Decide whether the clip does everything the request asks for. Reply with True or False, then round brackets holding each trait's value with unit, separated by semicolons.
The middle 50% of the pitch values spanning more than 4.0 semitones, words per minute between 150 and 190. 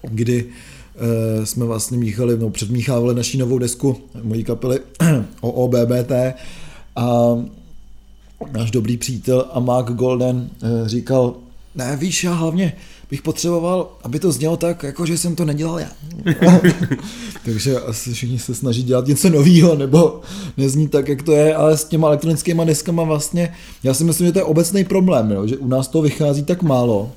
True (5.2 semitones; 165 wpm)